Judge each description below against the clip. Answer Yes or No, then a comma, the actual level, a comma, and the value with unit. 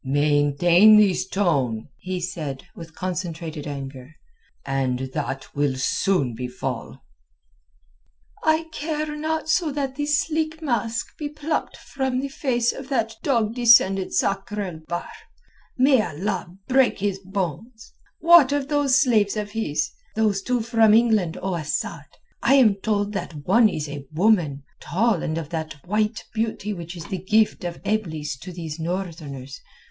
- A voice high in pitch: Yes, high, 200 Hz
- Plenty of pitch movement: Yes, wide, 7.1 semitones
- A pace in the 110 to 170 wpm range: Yes, average, 145 wpm